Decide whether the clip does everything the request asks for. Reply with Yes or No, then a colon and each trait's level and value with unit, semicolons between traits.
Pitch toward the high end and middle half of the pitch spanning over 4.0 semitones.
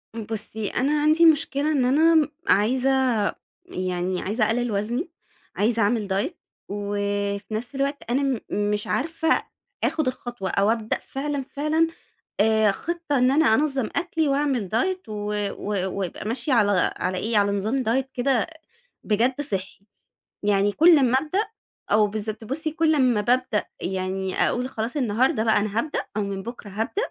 Yes: high, 235 Hz; wide, 5.5 semitones